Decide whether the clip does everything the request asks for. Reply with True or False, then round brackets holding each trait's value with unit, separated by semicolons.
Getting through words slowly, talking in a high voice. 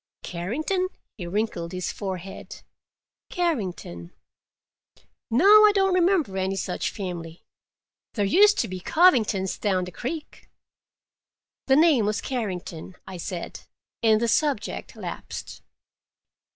True (110 wpm; 210 Hz)